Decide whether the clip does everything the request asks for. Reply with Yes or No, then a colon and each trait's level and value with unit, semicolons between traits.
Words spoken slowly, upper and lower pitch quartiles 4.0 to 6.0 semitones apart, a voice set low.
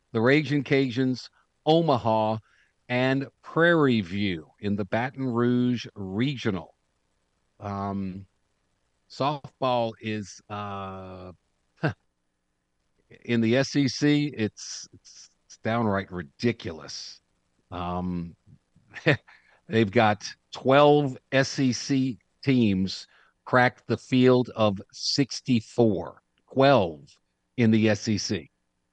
Yes: slow, 80 wpm; average, 5.3 semitones; low, 110 Hz